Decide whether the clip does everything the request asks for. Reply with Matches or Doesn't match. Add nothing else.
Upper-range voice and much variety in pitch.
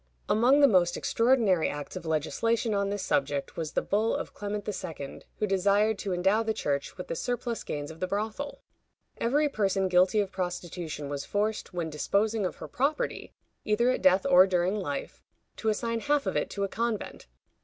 Doesn't match